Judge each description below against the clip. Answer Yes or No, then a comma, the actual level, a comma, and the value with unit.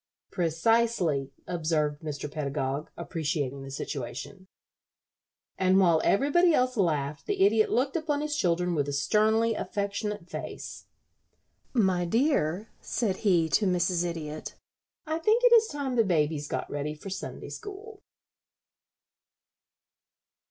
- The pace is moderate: No, slow, 125 wpm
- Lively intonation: Yes, wide, 7.2 semitones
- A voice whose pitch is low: No, medium, 180 Hz